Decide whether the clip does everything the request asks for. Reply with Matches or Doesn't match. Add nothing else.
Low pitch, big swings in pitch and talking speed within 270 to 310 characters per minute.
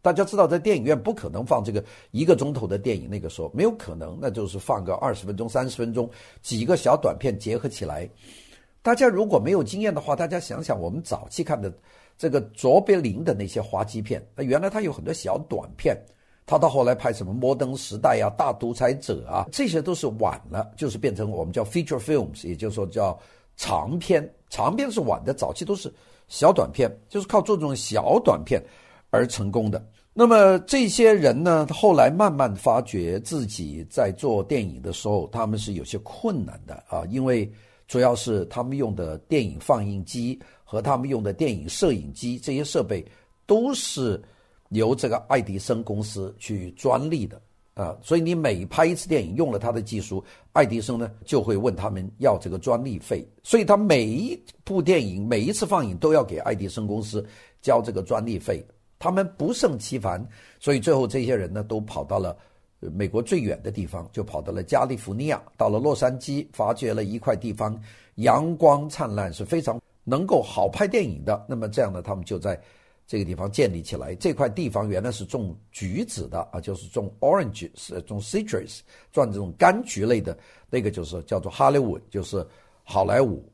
Matches